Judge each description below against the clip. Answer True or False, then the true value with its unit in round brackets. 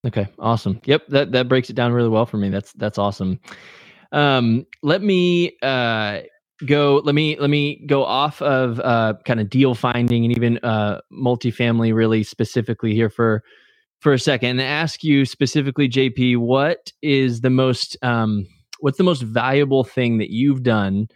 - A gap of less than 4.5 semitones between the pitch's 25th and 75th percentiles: True (3.7 semitones)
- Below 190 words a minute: True (175 wpm)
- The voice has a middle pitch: False (125 Hz)